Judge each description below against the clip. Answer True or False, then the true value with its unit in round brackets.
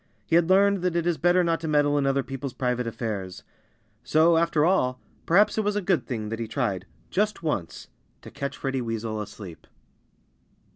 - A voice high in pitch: False (140 Hz)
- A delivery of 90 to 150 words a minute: False (190 wpm)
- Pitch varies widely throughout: True (6.8 semitones)